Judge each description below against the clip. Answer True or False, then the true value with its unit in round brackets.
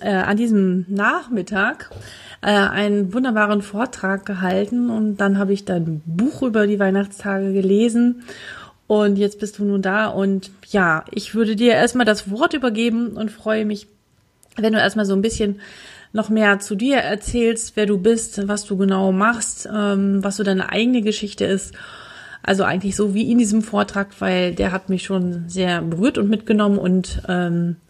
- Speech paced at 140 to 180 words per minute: True (170 wpm)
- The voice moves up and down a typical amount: False (2.0 semitones)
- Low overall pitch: False (205 Hz)